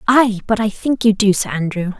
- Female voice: Yes, female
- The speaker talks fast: Yes, fast, 240 wpm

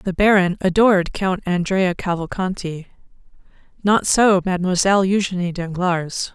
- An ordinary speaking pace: No, slow, 105 wpm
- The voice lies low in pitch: No, medium, 185 Hz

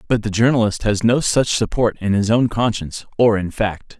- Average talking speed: No, fast, 210 wpm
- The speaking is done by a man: Yes, male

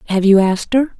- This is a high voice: Yes, high, 215 Hz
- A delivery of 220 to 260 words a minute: Yes, fast, 240 wpm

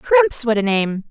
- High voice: Yes, high, 245 Hz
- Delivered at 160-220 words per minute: Yes, fast, 215 wpm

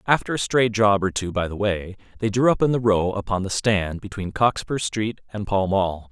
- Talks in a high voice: No, low, 105 Hz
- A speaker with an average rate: No, fast, 235 wpm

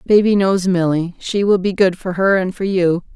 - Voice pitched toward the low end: No, medium, 185 Hz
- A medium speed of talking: No, fast, 230 wpm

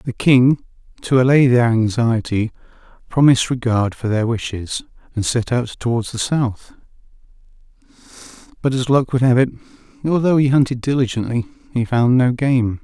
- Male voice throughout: Yes, male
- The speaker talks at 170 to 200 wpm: No, average, 145 wpm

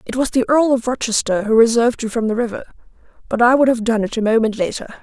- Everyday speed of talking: No, fast, 250 wpm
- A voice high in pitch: Yes, high, 235 Hz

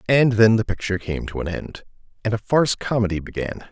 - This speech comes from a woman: No, male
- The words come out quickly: Yes, fast, 210 wpm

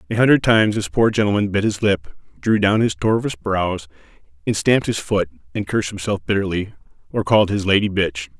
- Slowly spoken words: No, average, 195 wpm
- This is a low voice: Yes, low, 100 Hz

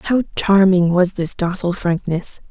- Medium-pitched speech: Yes, medium, 180 Hz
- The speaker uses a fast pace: No, average, 145 wpm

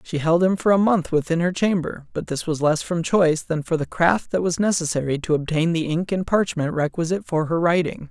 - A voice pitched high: No, medium, 170 Hz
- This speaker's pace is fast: Yes, fast, 235 wpm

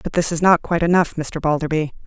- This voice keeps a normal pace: No, fast, 230 wpm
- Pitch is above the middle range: No, medium, 165 Hz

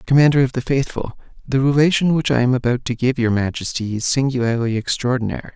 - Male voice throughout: Yes, male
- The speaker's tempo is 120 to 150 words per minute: No, average, 185 wpm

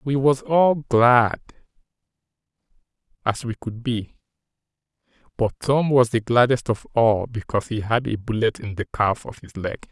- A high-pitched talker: No, low, 115 Hz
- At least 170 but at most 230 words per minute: No, average, 155 wpm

